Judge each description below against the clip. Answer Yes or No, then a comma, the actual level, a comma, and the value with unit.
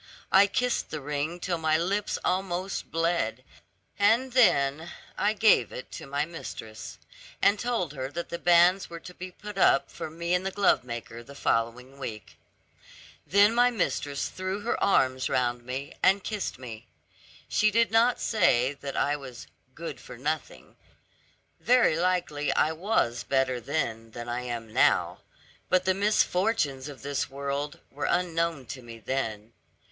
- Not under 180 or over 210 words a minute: No, average, 155 wpm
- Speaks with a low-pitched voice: No, medium, 155 Hz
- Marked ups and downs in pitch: Yes, wide, 6.5 semitones